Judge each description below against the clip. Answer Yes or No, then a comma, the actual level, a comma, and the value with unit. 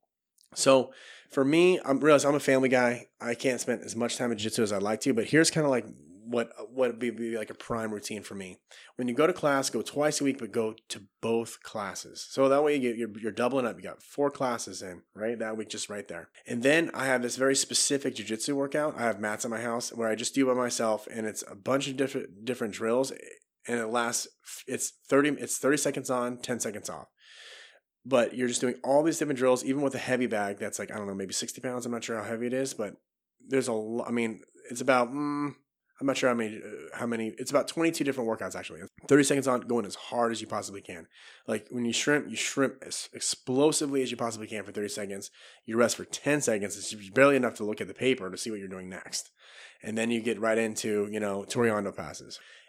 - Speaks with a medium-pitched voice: No, low, 120 Hz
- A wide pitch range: No, average, 3.6 semitones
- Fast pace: Yes, fast, 245 wpm